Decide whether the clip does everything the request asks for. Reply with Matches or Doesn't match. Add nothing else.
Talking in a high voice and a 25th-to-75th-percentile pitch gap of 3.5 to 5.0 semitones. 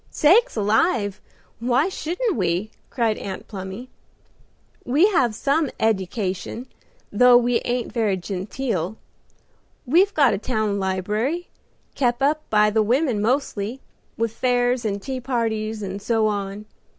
Matches